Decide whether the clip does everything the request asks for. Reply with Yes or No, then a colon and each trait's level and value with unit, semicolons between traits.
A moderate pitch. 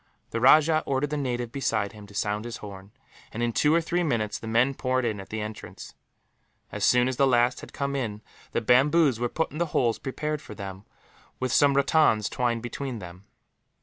No: low, 120 Hz